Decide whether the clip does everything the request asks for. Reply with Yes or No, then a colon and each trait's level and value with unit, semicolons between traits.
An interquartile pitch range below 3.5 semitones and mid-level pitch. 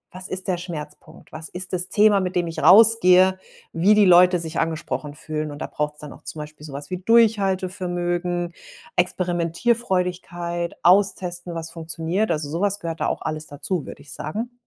Yes: narrow, 2.6 semitones; medium, 175 Hz